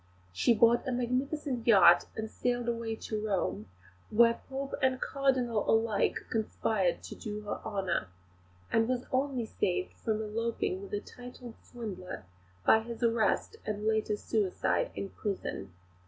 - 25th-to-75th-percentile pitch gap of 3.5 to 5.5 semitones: No, average, 2.8 semitones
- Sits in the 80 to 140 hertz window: No, high, 225 Hz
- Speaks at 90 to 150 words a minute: Yes, average, 140 wpm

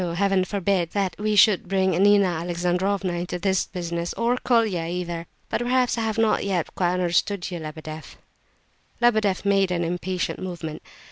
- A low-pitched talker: No, medium, 185 Hz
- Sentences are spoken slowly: No, average, 155 wpm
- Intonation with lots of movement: No, average, 2.7 semitones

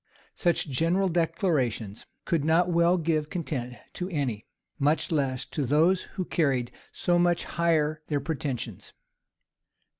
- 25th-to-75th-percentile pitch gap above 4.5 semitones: No, average, 4.0 semitones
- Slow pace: Yes, slow, 130 wpm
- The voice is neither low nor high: Yes, medium, 155 Hz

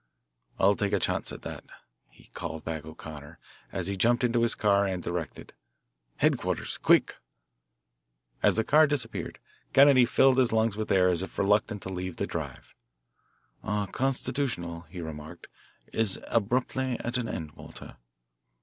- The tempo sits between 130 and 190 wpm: Yes, average, 150 wpm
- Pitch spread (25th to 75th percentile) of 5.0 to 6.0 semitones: Yes, wide, 5.6 semitones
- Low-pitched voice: Yes, low, 100 Hz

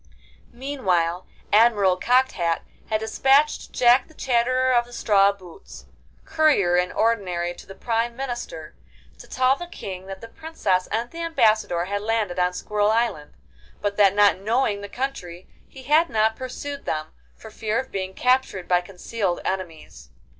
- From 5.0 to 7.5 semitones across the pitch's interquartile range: Yes, average, 5.3 semitones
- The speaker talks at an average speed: Yes, average, 160 wpm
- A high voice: Yes, high, 215 Hz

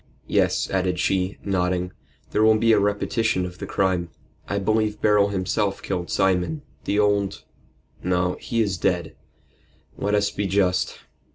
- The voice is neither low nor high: No, low, 100 Hz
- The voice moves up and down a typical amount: No, narrow, 2.3 semitones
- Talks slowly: No, average, 150 wpm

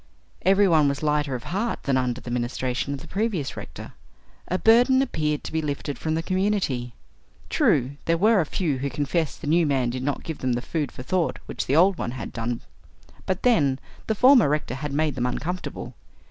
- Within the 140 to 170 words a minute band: No, fast, 205 wpm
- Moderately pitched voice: Yes, medium, 150 Hz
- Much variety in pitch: Yes, wide, 5.8 semitones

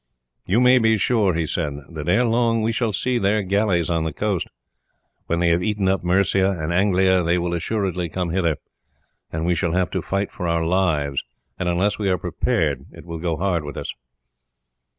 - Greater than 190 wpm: Yes, average, 200 wpm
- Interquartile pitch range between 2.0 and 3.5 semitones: Yes, average, 3.2 semitones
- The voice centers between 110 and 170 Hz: No, very low, 90 Hz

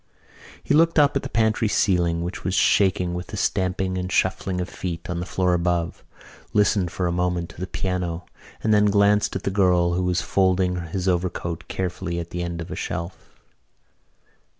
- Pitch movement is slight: Yes, narrow, 1.9 semitones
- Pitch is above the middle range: No, very low, 90 Hz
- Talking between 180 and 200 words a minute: Yes, average, 190 wpm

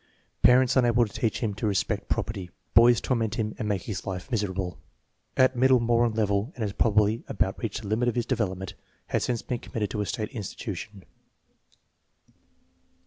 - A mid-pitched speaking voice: No, low, 110 Hz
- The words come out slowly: No, average, 175 wpm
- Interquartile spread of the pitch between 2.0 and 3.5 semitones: Yes, average, 2.8 semitones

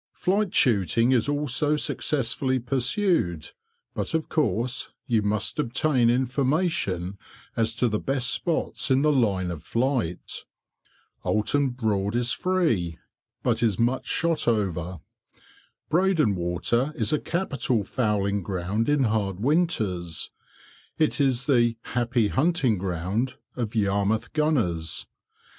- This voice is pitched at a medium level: No, low, 120 Hz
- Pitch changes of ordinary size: No, wide, 6.0 semitones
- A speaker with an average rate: No, slow, 120 wpm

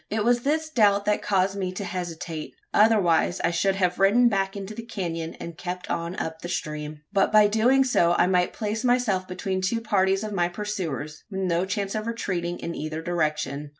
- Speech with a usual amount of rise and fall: Yes, average, 3.6 semitones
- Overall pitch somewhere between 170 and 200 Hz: Yes, high, 190 Hz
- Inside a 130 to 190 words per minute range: No, average, 200 wpm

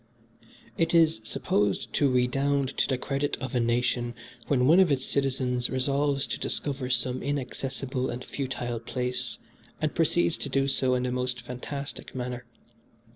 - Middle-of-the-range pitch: No, low, 130 Hz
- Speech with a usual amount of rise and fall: No, narrow, 2.0 semitones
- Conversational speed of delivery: Yes, average, 155 wpm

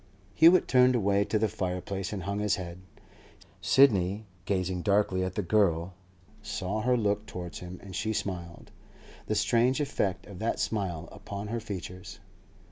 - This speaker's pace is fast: No, average, 155 wpm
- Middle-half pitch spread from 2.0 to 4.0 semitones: Yes, average, 3.0 semitones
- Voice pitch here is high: No, low, 100 Hz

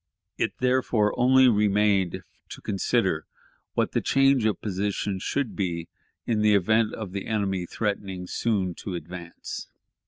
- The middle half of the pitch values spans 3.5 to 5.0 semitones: No, average, 3.0 semitones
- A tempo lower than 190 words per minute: Yes, slow, 135 wpm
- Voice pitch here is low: Yes, low, 105 Hz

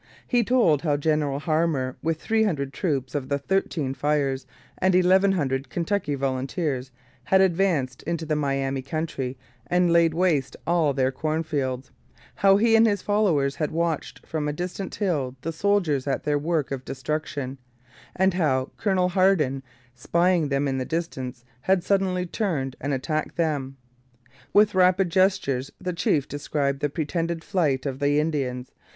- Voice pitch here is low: No, medium, 155 Hz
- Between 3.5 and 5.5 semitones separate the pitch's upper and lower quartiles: Yes, average, 4.8 semitones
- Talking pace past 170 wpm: No, average, 155 wpm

